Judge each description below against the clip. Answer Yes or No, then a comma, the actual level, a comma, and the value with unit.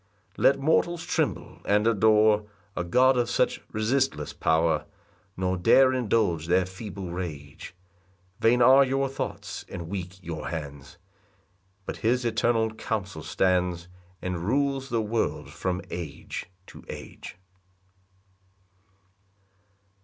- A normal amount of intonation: No, wide, 5.7 semitones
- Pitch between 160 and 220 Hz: No, low, 105 Hz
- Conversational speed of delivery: No, slow, 115 wpm